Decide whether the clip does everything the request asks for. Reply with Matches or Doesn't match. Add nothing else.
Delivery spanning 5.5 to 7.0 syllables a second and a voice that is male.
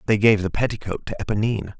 Doesn't match